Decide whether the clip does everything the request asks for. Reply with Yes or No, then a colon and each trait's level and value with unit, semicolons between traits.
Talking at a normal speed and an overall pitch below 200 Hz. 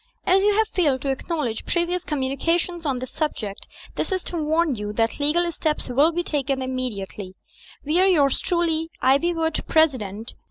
No: average, 170 wpm; very high, 300 Hz